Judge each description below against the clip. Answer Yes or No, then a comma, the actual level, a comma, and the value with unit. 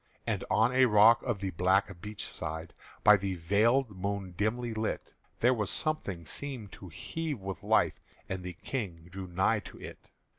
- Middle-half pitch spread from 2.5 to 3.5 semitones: No, average, 4.1 semitones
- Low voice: Yes, low, 100 Hz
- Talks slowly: No, average, 175 wpm